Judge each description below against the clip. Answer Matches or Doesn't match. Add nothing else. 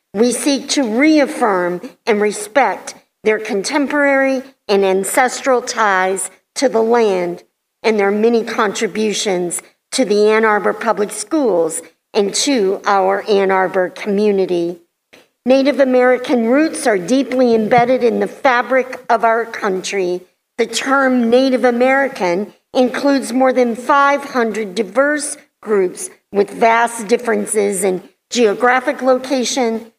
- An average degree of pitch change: Matches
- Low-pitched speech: Doesn't match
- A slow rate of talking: Matches